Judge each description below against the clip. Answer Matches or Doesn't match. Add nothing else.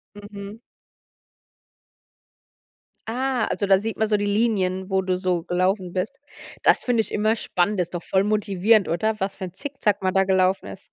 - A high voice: Matches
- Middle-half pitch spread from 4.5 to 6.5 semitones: Doesn't match